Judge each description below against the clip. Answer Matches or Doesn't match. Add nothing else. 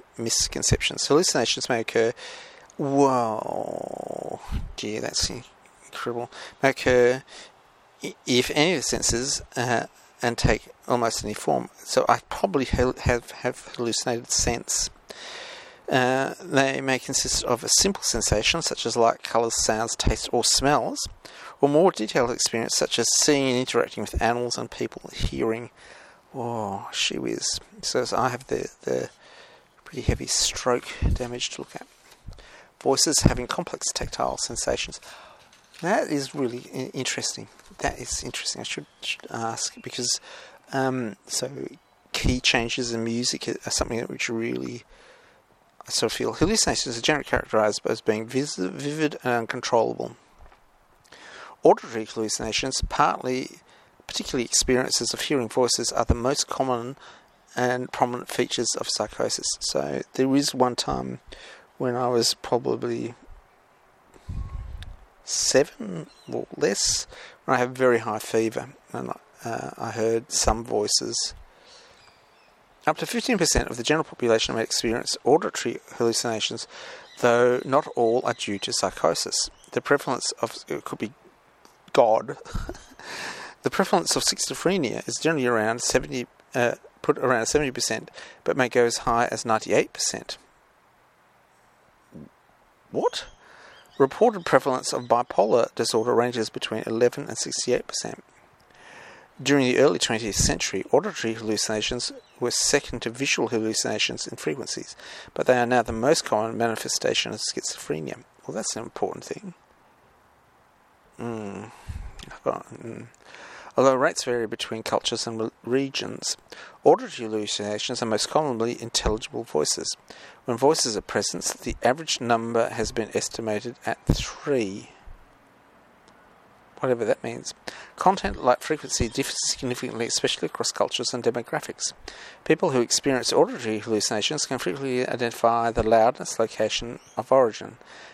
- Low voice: Matches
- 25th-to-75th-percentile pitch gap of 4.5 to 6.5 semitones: Doesn't match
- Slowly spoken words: Matches